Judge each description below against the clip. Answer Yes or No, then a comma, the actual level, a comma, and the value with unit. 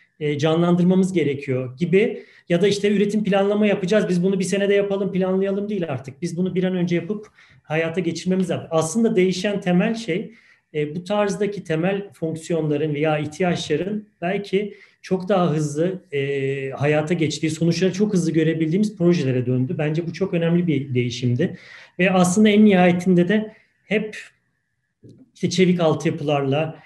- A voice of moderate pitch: Yes, medium, 175 Hz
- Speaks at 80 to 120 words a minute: No, fast, 140 wpm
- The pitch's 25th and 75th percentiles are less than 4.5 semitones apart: Yes, average, 4.0 semitones